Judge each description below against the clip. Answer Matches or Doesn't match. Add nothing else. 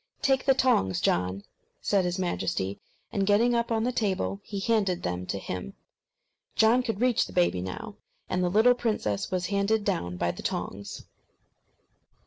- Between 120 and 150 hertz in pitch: Doesn't match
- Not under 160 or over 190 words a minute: Matches